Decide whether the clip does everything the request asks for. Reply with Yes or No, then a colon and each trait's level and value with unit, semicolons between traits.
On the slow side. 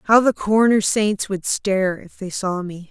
No: fast, 205 wpm